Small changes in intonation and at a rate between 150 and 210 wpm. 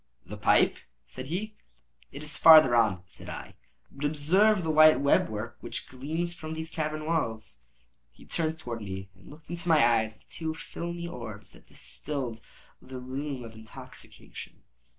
No: wide, 5.6 semitones; average, 165 wpm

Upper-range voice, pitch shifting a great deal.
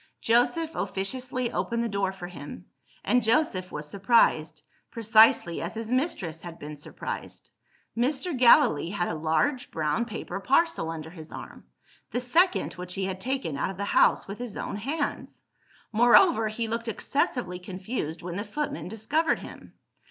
Yes: high, 215 Hz; wide, 5.9 semitones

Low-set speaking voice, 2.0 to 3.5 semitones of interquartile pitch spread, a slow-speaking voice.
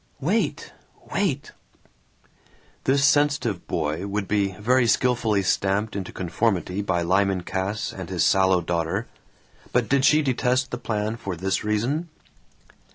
No: low, 105 Hz; average, 5.1 semitones; slow, 130 wpm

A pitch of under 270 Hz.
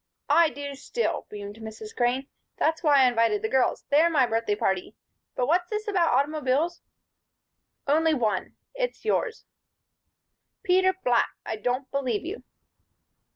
No: very high, 275 Hz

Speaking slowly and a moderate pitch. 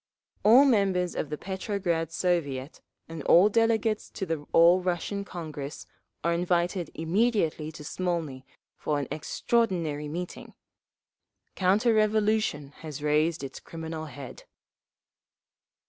Yes: slow, 115 wpm; medium, 170 Hz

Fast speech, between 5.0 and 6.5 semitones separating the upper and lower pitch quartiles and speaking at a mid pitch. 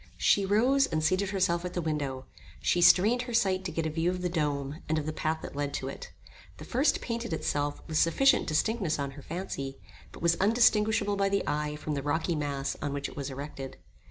Yes: fast, 220 wpm; average, 5.3 semitones; medium, 165 Hz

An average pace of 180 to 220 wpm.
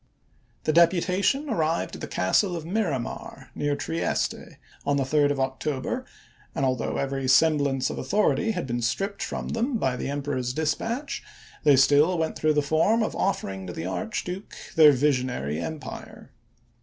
No: average, 160 wpm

